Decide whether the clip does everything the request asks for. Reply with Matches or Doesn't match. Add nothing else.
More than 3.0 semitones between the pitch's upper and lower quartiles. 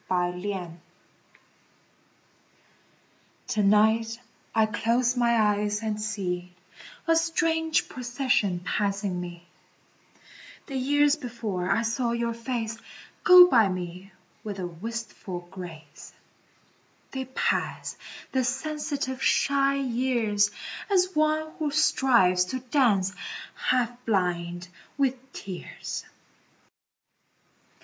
Matches